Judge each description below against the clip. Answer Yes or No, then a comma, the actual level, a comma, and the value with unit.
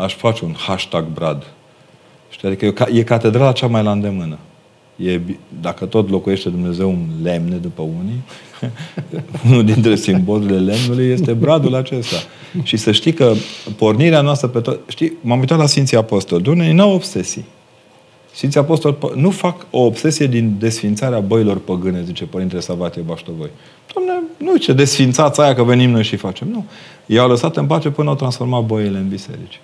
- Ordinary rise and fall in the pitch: No, wide, 7.1 semitones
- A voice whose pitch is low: Yes, low, 115 Hz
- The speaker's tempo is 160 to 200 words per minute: Yes, average, 165 wpm